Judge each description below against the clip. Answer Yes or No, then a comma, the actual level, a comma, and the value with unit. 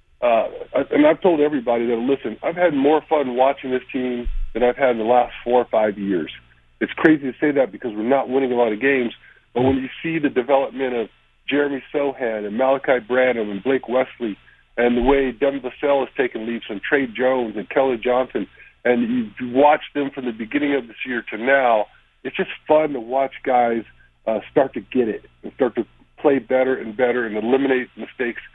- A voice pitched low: Yes, low, 130 Hz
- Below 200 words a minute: No, fast, 205 wpm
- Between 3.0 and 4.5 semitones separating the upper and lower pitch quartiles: No, narrow, 2.5 semitones